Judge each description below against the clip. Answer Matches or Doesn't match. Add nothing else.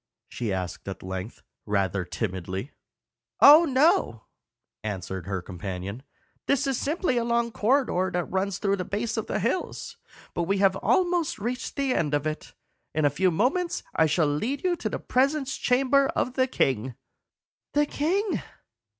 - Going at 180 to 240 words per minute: Doesn't match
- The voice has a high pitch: Matches